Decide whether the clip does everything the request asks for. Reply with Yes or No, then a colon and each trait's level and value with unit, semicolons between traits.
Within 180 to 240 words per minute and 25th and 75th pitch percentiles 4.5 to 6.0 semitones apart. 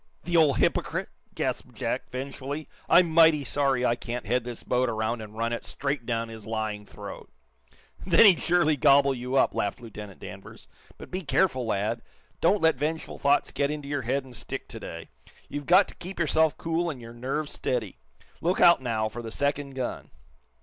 Yes: average, 190 wpm; average, 5.0 semitones